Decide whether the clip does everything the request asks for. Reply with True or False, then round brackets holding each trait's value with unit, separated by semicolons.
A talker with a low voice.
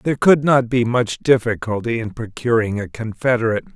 True (120 Hz)